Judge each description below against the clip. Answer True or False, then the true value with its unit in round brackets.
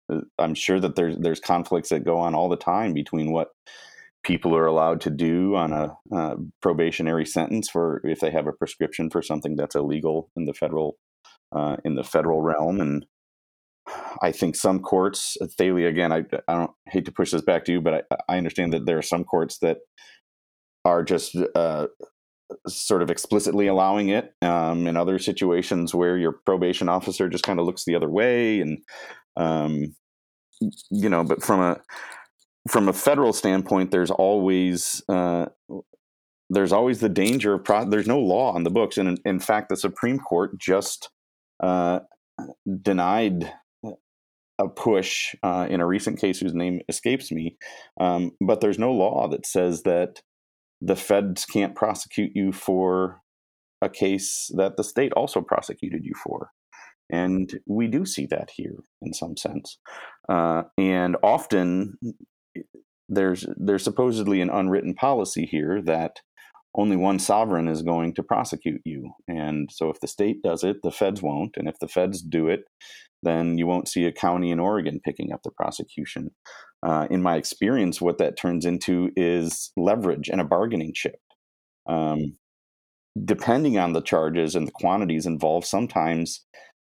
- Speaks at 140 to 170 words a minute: True (165 wpm)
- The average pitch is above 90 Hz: False (85 Hz)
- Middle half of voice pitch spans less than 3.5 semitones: True (2.9 semitones)